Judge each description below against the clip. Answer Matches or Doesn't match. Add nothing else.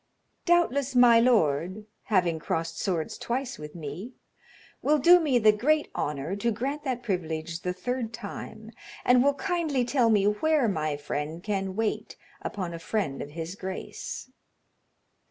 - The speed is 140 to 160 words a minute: Matches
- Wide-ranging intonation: Matches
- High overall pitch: Matches